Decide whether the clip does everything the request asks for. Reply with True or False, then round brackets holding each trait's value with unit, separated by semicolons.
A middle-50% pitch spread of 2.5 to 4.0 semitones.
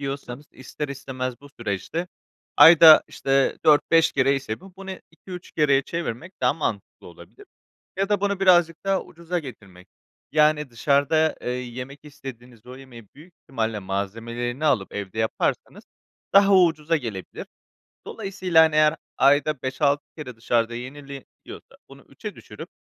False (5.1 semitones)